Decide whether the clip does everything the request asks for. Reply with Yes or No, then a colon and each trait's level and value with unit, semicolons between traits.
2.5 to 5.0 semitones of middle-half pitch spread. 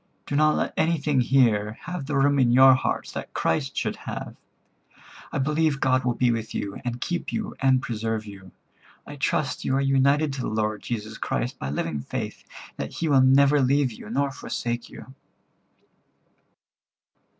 Yes: average, 3.6 semitones